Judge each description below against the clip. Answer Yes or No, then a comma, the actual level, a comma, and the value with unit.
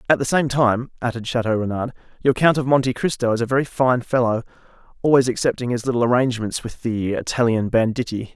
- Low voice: Yes, low, 120 Hz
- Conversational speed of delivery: Yes, average, 185 wpm